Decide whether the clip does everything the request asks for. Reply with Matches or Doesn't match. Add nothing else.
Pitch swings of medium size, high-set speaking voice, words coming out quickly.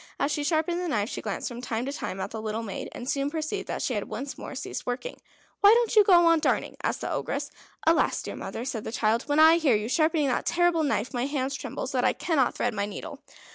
Doesn't match